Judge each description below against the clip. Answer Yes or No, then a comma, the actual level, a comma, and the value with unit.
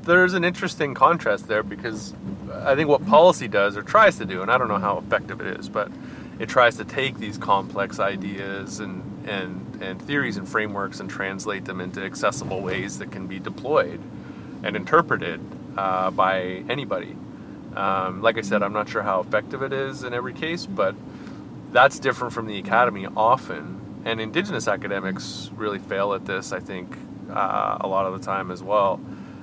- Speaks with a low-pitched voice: Yes, low, 100 Hz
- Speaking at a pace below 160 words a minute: No, average, 185 wpm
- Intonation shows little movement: No, average, 3.2 semitones